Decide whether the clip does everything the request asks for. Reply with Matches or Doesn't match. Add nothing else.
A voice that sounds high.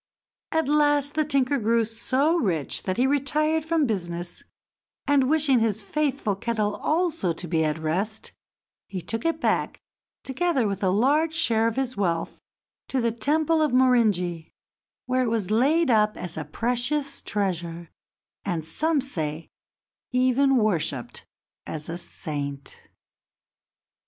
Matches